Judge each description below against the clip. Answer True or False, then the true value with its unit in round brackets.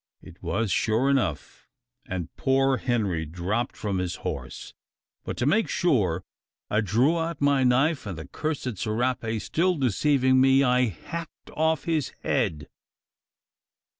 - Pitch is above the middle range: False (125 Hz)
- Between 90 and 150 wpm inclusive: True (140 wpm)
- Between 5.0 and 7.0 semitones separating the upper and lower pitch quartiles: True (5.5 semitones)